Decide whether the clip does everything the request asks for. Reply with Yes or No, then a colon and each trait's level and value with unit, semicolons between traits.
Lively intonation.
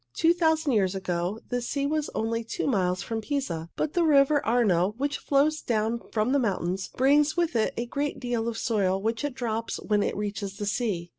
Yes: wide, 5.7 semitones